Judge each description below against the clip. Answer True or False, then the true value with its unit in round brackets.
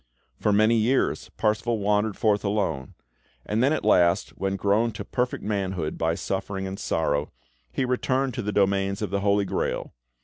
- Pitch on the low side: True (100 Hz)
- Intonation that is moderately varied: False (2.2 semitones)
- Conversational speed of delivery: True (170 wpm)